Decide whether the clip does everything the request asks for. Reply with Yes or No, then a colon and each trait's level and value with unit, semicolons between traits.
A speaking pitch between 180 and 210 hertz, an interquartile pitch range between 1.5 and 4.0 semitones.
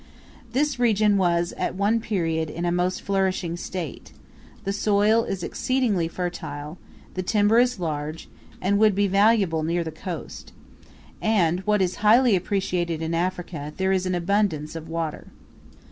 Yes: medium, 185 Hz; average, 3.7 semitones